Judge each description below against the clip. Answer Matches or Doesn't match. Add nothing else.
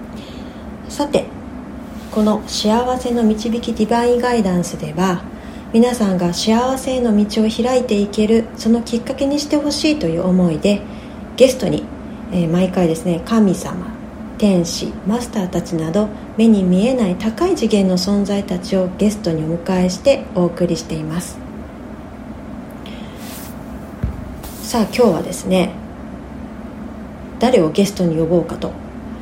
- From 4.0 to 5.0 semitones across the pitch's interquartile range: Matches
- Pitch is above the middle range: Matches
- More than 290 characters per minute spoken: Doesn't match